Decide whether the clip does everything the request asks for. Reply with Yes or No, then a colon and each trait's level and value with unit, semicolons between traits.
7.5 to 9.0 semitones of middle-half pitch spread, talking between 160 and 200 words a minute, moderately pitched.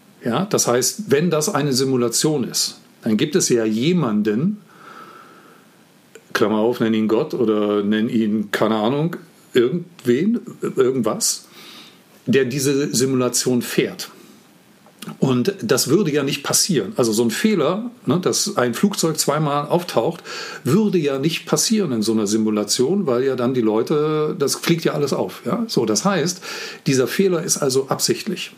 No: wide, 8.7 semitones; average, 150 wpm; medium, 155 Hz